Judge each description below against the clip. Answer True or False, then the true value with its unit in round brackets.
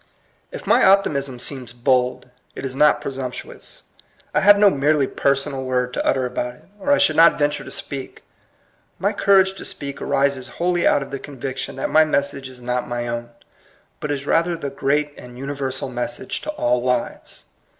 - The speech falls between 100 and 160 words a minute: False (180 wpm)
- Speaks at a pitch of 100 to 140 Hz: True (135 Hz)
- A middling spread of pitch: True (3.0 semitones)